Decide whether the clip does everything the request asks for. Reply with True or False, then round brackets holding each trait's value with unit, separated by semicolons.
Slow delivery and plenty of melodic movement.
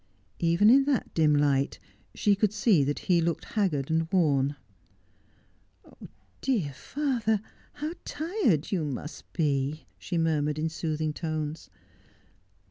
True (125 wpm; 5.9 semitones)